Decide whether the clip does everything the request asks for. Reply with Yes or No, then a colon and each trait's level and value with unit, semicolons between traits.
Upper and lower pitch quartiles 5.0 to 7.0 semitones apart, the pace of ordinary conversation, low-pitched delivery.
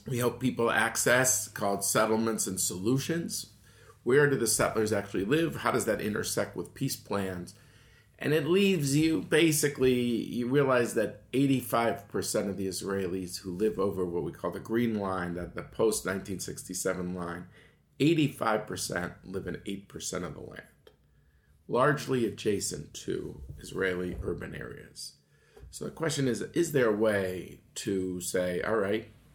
Yes: wide, 5.4 semitones; average, 145 wpm; low, 110 Hz